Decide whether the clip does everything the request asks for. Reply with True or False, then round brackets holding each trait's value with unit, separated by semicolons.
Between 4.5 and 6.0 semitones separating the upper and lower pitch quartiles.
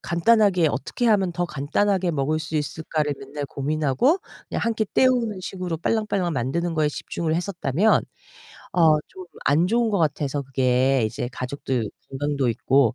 True (5.6 semitones)